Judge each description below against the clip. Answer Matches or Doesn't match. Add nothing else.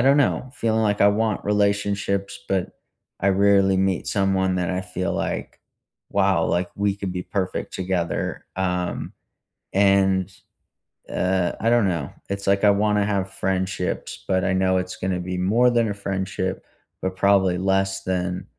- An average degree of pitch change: Doesn't match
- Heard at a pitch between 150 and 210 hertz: Doesn't match